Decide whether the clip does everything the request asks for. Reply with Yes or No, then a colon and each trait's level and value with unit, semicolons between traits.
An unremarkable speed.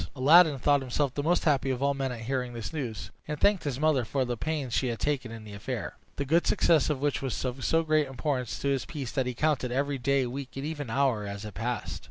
No: fast, 255 wpm